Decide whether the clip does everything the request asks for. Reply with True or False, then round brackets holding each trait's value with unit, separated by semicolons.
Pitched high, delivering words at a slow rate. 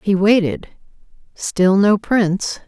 True (200 Hz; 110 wpm)